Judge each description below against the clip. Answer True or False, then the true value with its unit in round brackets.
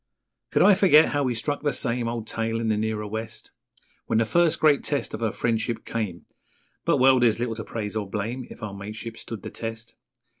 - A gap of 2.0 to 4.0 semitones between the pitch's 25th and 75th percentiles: True (2.5 semitones)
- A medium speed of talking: False (215 wpm)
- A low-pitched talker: True (115 Hz)